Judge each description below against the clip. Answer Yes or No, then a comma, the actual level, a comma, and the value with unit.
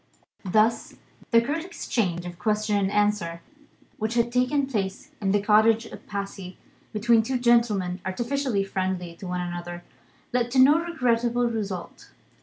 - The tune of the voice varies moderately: Yes, average, 4.1 semitones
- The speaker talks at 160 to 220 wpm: No, average, 145 wpm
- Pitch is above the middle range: Yes, high, 215 Hz